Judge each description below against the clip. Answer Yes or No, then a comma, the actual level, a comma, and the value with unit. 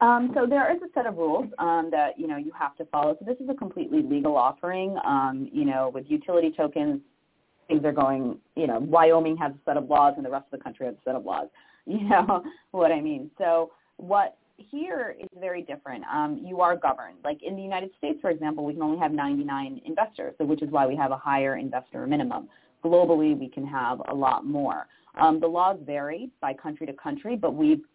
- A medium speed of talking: No, fast, 230 wpm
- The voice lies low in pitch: No, medium, 165 Hz